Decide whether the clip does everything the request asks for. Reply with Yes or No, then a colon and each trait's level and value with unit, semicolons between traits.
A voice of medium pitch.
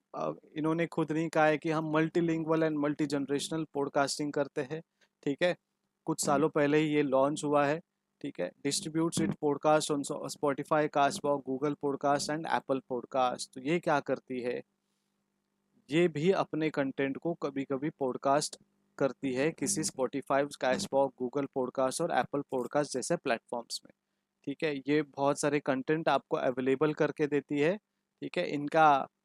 Yes: medium, 150 Hz